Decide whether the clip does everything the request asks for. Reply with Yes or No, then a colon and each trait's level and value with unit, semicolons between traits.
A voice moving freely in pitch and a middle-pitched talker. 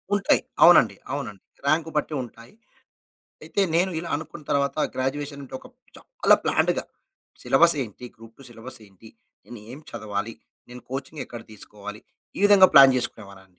No: wide, 5.7 semitones; low, 130 Hz